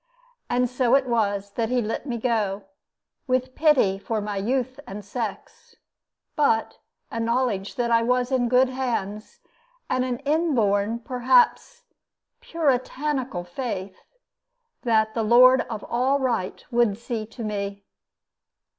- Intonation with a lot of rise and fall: No, average, 3.4 semitones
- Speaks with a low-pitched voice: No, high, 235 Hz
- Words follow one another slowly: Yes, slow, 130 wpm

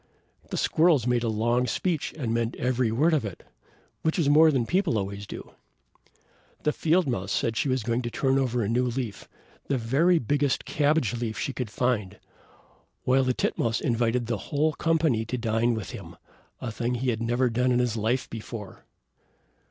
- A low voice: Yes, low, 125 Hz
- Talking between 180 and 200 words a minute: Yes, average, 190 wpm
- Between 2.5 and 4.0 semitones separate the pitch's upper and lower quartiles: Yes, average, 3.5 semitones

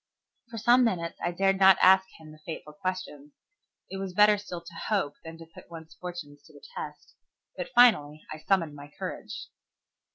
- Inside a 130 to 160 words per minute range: No, average, 185 wpm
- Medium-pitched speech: Yes, medium, 175 Hz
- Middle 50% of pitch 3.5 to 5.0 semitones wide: Yes, average, 3.8 semitones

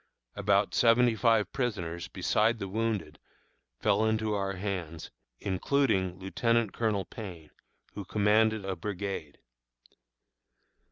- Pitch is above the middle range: No, low, 105 Hz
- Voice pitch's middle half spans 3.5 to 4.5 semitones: No, average, 2.9 semitones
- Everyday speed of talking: No, slow, 105 wpm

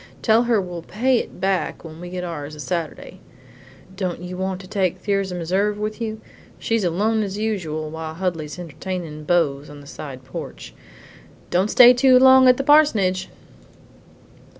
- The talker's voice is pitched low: No, medium, 185 Hz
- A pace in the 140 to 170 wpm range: Yes, average, 165 wpm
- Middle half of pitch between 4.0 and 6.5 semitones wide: Yes, average, 4.6 semitones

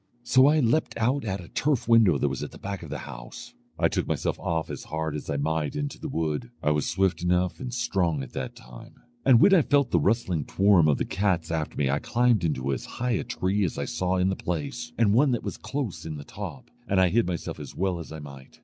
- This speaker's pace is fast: Yes, fast, 255 wpm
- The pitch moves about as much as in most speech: No, wide, 7.3 semitones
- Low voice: Yes, very low, 90 Hz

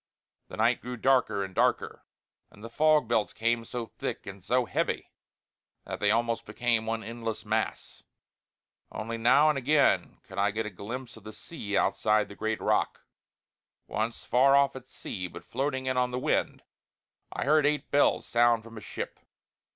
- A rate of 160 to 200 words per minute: Yes, average, 180 wpm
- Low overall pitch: Yes, low, 115 Hz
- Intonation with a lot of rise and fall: No, average, 3.1 semitones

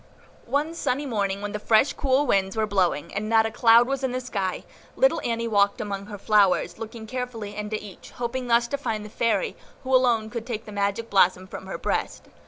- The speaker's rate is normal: No, fast, 210 wpm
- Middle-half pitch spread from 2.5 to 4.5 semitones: Yes, average, 3.6 semitones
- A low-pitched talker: No, high, 220 Hz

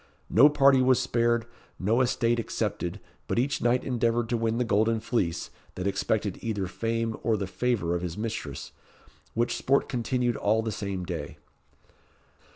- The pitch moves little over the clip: No, average, 3.0 semitones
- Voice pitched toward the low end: Yes, low, 115 Hz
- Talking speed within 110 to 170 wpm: Yes, average, 160 wpm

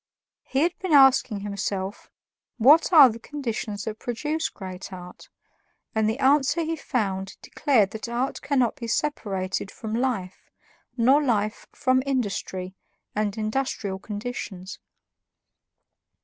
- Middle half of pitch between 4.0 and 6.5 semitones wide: Yes, average, 5.1 semitones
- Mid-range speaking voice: No, high, 230 Hz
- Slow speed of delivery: Yes, slow, 120 wpm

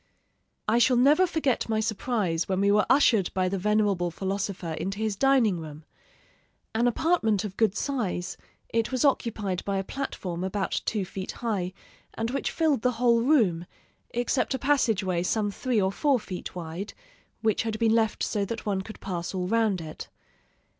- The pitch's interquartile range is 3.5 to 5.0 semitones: Yes, average, 4.1 semitones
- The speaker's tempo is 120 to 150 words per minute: No, average, 175 wpm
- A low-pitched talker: No, high, 215 Hz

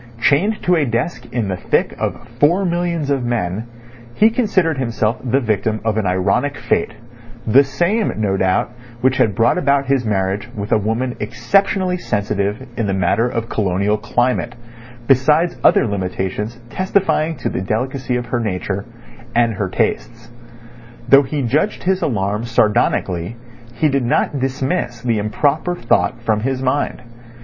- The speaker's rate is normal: Yes, average, 150 wpm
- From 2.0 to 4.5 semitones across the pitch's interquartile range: No, average, 5.0 semitones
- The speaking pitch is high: No, low, 120 Hz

